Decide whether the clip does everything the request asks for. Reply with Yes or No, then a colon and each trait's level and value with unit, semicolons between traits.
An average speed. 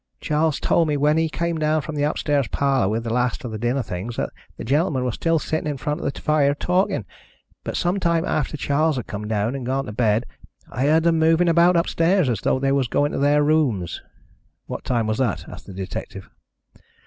No: fast, 220 wpm